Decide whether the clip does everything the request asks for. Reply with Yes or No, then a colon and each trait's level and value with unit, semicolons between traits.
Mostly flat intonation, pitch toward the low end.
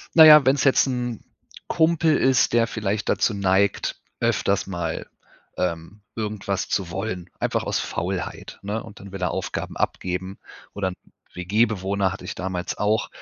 No: average, 3.4 semitones; low, 100 Hz